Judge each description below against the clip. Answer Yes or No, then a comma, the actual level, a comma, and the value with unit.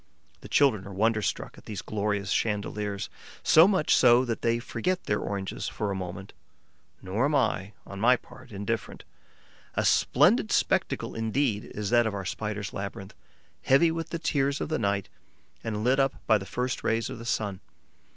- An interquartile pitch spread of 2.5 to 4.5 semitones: Yes, average, 4.1 semitones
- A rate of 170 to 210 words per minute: Yes, average, 175 wpm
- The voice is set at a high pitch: No, low, 110 Hz